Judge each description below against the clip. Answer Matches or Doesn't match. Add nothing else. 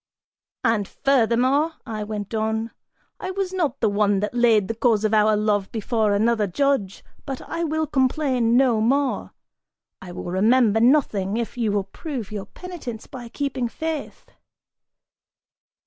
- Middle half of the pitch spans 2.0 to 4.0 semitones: Doesn't match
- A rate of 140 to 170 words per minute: Matches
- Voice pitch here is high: Matches